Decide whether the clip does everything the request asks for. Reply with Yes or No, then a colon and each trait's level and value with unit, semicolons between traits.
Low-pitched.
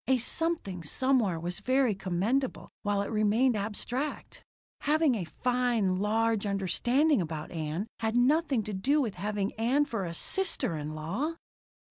No: high, 220 Hz